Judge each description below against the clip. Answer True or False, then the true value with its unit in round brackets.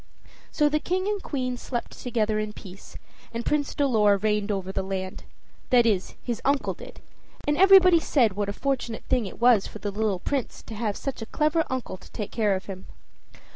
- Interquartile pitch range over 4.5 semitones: True (5.2 semitones)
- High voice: True (230 Hz)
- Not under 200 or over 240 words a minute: True (205 wpm)